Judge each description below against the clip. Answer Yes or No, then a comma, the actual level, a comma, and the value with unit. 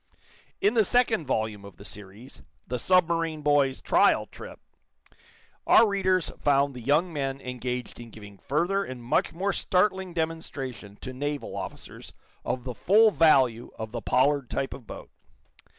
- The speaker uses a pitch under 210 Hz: Yes, medium, 140 Hz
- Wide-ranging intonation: Yes, wide, 5.8 semitones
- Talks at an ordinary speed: Yes, average, 150 wpm